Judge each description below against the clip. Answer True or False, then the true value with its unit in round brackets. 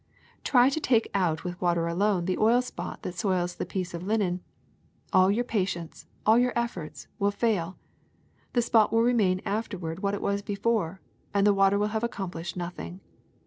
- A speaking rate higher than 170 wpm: True (180 wpm)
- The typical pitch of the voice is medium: False (200 Hz)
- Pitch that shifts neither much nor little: True (3.9 semitones)